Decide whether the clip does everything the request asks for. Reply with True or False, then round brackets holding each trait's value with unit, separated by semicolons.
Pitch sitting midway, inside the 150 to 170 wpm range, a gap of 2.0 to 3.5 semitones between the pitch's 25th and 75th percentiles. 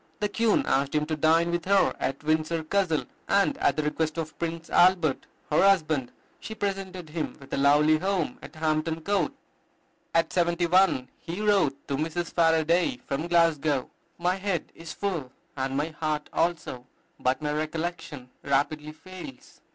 True (160 Hz; 160 wpm; 2.9 semitones)